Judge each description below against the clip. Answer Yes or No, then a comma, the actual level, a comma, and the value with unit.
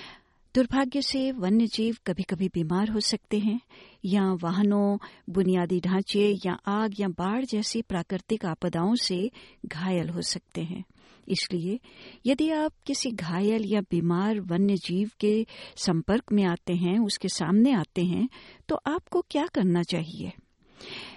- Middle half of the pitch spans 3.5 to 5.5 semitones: Yes, average, 3.9 semitones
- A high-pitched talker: Yes, high, 200 Hz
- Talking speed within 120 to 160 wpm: Yes, average, 140 wpm